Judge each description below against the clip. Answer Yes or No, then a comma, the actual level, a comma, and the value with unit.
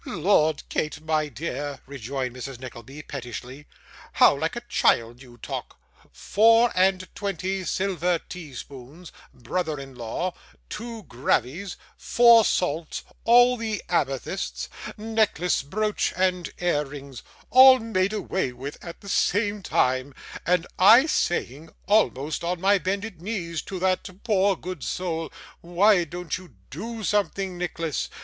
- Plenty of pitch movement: Yes, wide, 6.0 semitones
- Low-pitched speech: No, medium, 175 Hz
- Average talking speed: No, slow, 130 wpm